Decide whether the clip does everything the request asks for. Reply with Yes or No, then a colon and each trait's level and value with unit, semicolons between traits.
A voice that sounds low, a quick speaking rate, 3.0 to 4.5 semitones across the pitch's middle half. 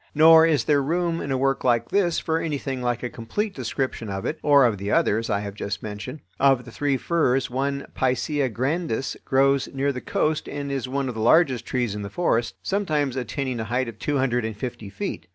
Yes: low, 130 Hz; fast, 220 wpm; average, 3.6 semitones